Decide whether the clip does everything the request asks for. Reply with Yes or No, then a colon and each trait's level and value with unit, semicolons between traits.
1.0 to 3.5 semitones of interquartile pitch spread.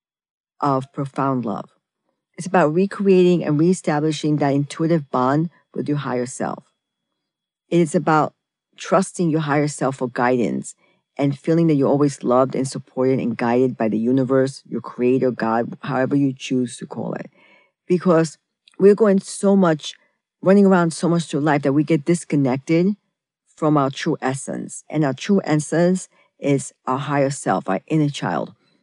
No: average, 4.2 semitones